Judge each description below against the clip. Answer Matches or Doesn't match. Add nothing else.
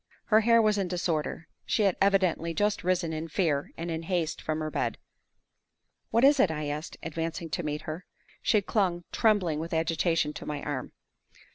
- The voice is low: Doesn't match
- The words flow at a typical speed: Matches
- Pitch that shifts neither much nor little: Matches